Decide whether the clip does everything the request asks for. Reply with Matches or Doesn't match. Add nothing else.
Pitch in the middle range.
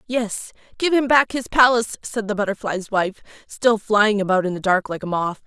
Doesn't match